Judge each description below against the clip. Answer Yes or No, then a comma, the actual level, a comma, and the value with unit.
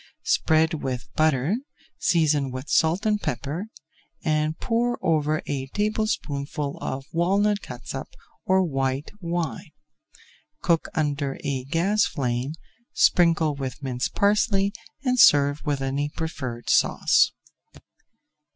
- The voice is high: No, medium, 155 Hz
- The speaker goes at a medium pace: No, slow, 110 wpm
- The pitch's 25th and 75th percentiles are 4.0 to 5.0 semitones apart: Yes, average, 4.7 semitones